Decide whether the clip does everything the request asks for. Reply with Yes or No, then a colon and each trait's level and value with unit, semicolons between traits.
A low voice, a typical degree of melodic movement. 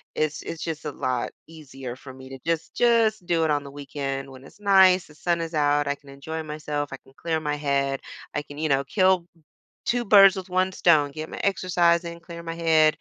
No: medium, 155 Hz; average, 3.5 semitones